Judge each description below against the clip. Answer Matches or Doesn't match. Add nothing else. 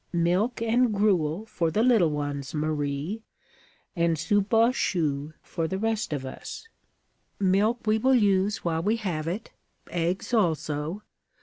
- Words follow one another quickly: Doesn't match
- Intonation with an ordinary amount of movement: Doesn't match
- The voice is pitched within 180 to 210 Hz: Matches